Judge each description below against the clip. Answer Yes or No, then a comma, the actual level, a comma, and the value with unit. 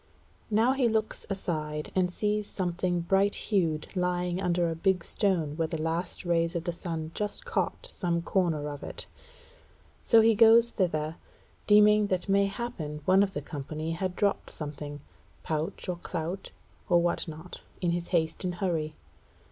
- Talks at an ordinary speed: Yes, average, 160 wpm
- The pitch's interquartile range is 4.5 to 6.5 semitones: No, average, 3.5 semitones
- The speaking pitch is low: No, medium, 175 Hz